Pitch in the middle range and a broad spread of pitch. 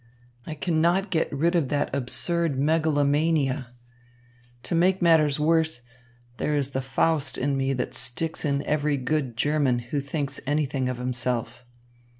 No: medium, 145 Hz; average, 3.2 semitones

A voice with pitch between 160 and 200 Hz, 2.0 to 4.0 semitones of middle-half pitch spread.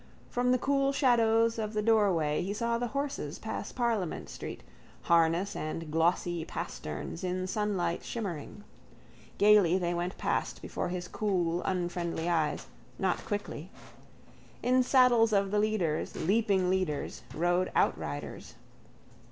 No: high, 190 Hz; average, 4.6 semitones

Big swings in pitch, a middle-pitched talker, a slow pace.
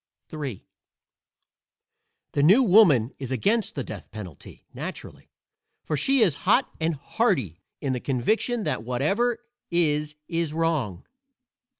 Yes: wide, 8.0 semitones; medium, 150 Hz; slow, 120 wpm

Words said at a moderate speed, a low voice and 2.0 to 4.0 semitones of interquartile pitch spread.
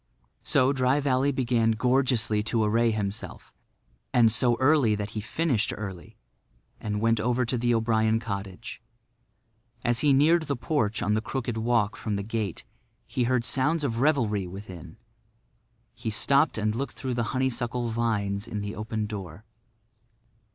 Yes: average, 150 wpm; low, 115 Hz; average, 3.2 semitones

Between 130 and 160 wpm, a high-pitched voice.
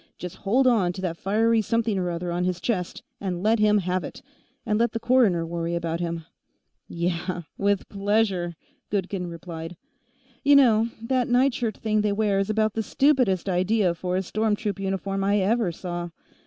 No: average, 180 wpm; high, 195 Hz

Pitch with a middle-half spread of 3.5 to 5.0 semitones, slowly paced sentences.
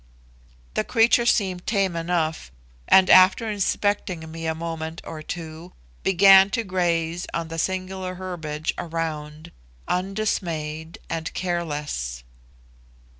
No: average, 2.8 semitones; slow, 110 wpm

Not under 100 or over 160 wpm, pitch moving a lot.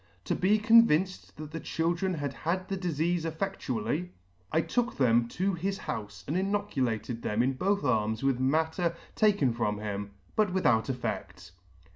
Yes: average, 155 wpm; wide, 7.8 semitones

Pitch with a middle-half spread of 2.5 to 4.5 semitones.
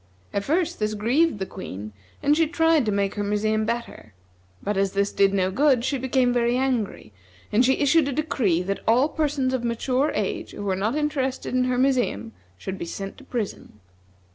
No: wide, 5.6 semitones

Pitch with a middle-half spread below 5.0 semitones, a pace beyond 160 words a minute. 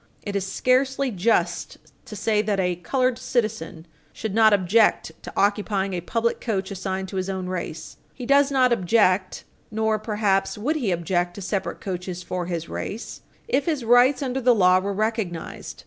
Yes: average, 4.1 semitones; average, 175 wpm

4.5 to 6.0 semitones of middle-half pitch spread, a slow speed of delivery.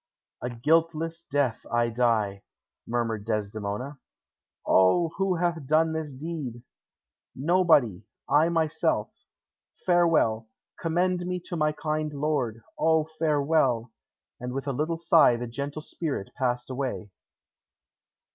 Yes: wide, 5.5 semitones; slow, 115 wpm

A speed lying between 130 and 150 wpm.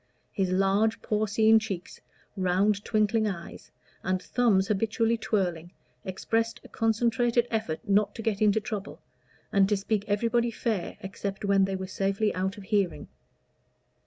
Yes: average, 140 wpm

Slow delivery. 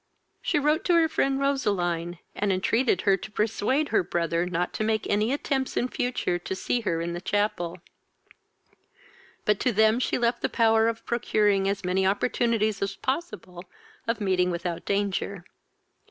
No: average, 165 wpm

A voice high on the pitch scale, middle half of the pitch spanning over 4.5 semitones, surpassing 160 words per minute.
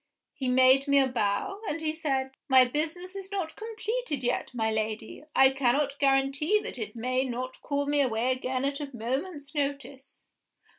No: very high, 275 Hz; average, 3.0 semitones; average, 170 wpm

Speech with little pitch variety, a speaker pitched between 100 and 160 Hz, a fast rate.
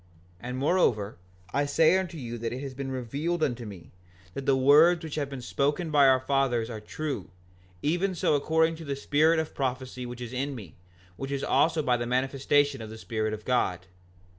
No: average, 3.9 semitones; low, 135 Hz; fast, 210 wpm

